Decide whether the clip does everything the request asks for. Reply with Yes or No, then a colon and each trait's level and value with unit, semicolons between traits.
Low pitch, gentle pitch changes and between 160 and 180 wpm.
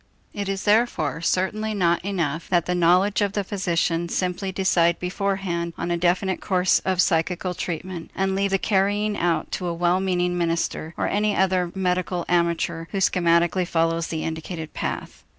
No: medium, 180 Hz; narrow, 2.2 semitones; average, 170 wpm